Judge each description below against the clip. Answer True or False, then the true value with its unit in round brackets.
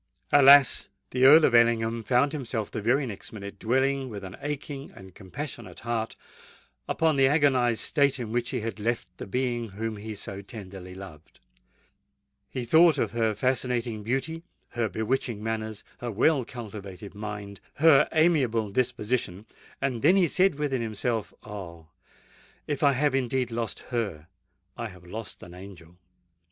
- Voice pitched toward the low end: True (115 Hz)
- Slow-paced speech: False (145 wpm)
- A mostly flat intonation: False (4.3 semitones)